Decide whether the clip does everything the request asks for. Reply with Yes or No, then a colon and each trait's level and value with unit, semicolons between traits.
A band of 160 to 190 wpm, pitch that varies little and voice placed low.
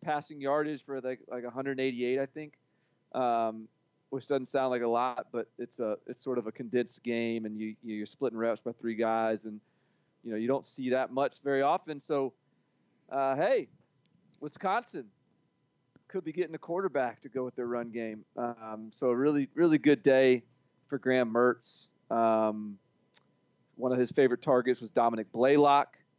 No: average, 175 wpm; average, 3.2 semitones; low, 125 Hz